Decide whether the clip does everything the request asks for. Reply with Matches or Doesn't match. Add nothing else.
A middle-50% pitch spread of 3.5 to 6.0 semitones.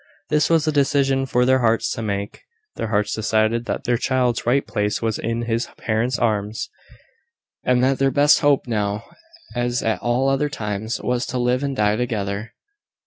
Doesn't match